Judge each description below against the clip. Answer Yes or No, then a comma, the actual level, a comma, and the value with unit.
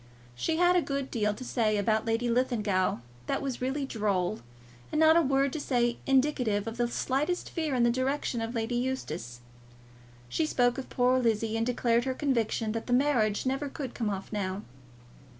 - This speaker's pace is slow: No, average, 185 wpm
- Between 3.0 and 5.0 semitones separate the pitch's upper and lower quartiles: Yes, average, 3.7 semitones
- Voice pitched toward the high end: Yes, high, 245 Hz